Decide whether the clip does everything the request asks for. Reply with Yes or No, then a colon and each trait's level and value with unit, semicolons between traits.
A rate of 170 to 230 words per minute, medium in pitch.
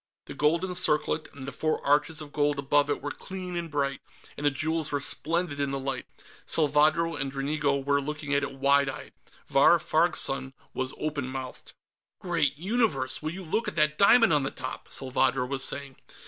Yes: average, 190 wpm; medium, 145 Hz